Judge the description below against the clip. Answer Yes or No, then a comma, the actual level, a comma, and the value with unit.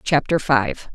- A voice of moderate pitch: Yes, medium, 150 Hz